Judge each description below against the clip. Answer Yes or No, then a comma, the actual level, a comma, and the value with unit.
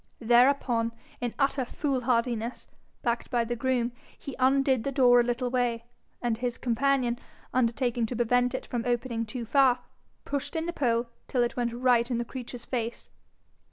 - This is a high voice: Yes, high, 245 Hz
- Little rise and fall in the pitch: Yes, narrow, 1.6 semitones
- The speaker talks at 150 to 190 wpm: Yes, average, 170 wpm